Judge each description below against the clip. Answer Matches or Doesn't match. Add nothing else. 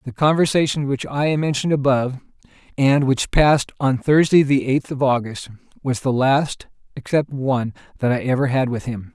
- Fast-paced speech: Doesn't match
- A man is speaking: Matches